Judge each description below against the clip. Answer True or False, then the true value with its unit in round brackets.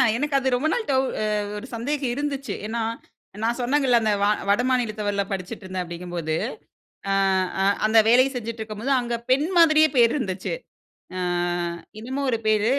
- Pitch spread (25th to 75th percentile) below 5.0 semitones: True (4.2 semitones)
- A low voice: False (235 Hz)